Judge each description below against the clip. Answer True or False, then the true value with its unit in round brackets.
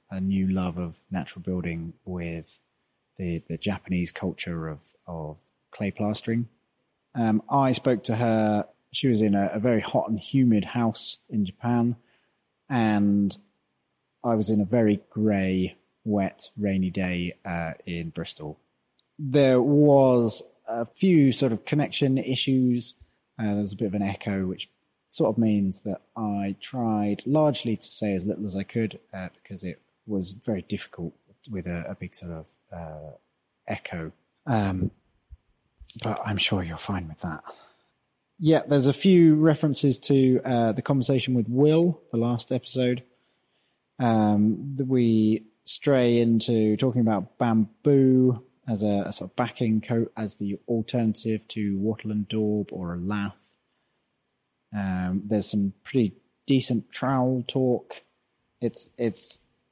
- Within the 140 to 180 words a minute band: True (145 wpm)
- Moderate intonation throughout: True (4.3 semitones)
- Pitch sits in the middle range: False (110 Hz)